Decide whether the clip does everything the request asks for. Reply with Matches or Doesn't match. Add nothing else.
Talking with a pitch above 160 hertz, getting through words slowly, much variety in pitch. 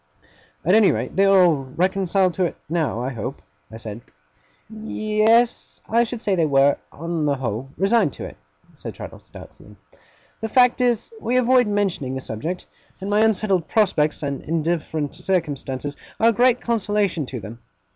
Doesn't match